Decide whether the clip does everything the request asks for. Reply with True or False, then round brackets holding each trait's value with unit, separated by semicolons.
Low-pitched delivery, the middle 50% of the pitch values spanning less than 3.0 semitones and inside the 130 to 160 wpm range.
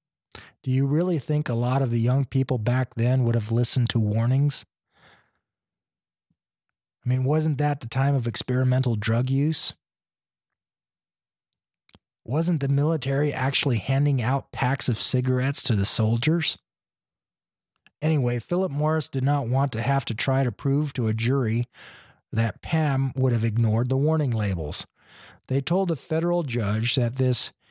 False (130 Hz; 3.4 semitones; 150 wpm)